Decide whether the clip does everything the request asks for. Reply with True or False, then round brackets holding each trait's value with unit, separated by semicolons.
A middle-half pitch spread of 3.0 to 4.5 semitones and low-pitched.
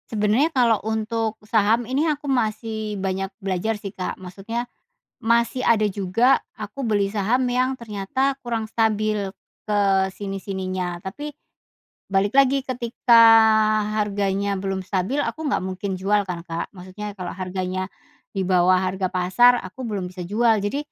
False (3.6 semitones; 210 Hz)